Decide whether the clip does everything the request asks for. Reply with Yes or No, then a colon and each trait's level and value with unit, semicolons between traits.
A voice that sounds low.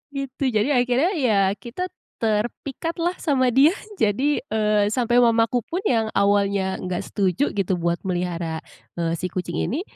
No: high, 220 Hz